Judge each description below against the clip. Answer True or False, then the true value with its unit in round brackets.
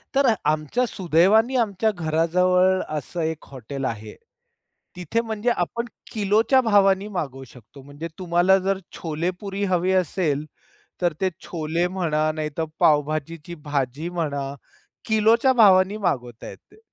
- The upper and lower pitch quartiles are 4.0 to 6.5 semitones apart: True (4.6 semitones)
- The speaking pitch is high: False (175 Hz)